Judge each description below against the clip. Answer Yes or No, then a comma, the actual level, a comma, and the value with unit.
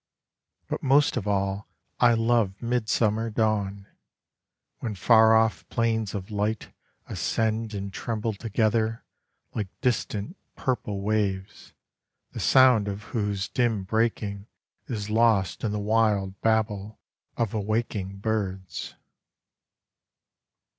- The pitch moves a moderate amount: No, narrow, 2.1 semitones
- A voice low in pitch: Yes, low, 110 Hz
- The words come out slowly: Yes, slow, 105 wpm